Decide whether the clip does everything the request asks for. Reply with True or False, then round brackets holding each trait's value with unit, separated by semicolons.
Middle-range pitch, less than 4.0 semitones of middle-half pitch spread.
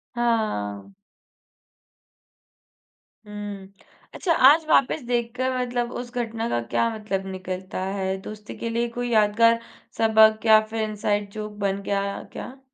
False (220 Hz; 3.0 semitones)